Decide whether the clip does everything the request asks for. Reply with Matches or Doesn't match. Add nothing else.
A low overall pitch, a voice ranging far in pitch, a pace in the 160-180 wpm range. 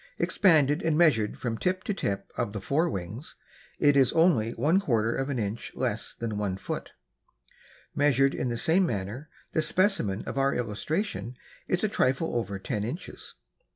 Matches